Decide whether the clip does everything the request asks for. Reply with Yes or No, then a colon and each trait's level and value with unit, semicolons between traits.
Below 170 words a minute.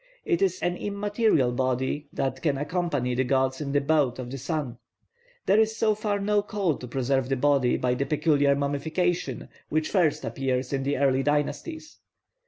No: average, 180 wpm